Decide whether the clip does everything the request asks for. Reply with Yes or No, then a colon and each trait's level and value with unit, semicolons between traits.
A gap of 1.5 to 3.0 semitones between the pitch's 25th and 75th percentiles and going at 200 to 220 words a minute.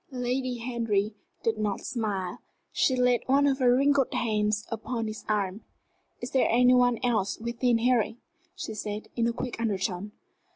No: average, 2.7 semitones; average, 160 wpm